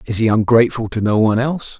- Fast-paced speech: Yes, fast, 235 wpm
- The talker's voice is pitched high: No, low, 115 Hz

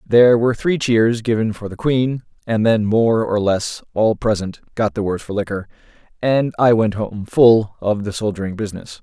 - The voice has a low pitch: Yes, low, 110 Hz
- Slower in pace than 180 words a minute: No, average, 195 wpm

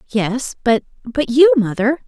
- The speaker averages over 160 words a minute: No, slow, 85 wpm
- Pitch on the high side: Yes, very high, 250 Hz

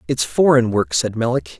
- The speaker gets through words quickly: No, average, 190 wpm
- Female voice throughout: No, male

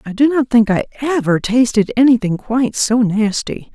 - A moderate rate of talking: Yes, average, 175 wpm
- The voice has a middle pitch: No, high, 235 Hz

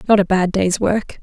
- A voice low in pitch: No, high, 195 Hz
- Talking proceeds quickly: Yes, fast, 245 wpm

